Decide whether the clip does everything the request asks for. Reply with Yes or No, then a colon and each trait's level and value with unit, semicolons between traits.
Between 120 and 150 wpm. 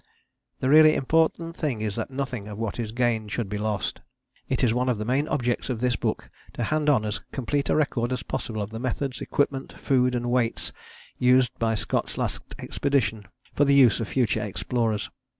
No: average, 200 wpm